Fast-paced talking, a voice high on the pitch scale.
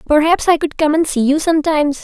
Yes: fast, 235 wpm; very high, 305 Hz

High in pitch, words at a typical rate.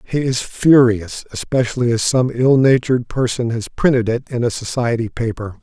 No: low, 120 Hz; average, 170 wpm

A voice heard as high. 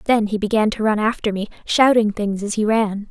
Yes: high, 215 Hz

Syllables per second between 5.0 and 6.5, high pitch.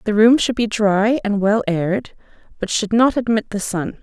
No: 4.7 syllables/s; high, 210 Hz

